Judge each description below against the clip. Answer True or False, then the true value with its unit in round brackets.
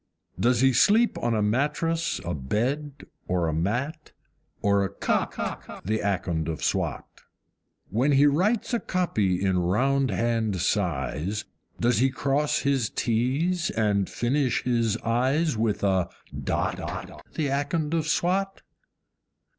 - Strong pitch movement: True (6.5 semitones)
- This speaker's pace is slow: True (130 wpm)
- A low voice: True (120 Hz)